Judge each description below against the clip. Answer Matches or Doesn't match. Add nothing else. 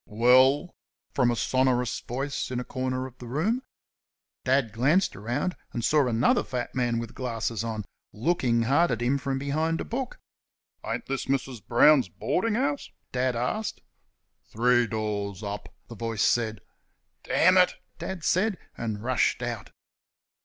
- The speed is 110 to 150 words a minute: Matches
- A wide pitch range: Doesn't match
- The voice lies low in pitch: Matches